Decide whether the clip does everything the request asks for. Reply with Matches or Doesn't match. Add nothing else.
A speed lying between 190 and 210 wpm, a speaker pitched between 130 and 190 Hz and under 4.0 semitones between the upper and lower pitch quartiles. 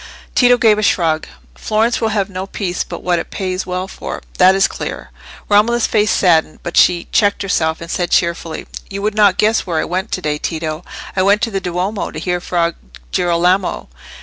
Matches